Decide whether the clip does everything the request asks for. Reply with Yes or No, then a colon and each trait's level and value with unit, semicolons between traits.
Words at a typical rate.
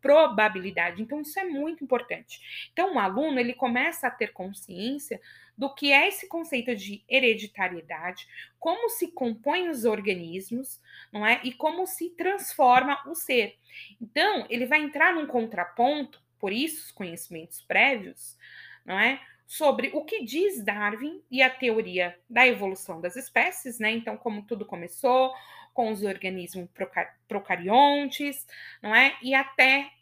Yes: average, 145 wpm